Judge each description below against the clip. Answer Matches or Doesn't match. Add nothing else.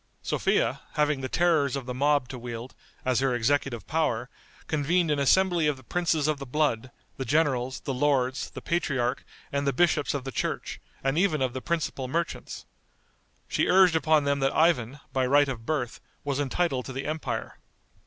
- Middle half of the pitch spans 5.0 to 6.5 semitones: Doesn't match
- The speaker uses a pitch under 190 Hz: Matches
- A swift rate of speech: Doesn't match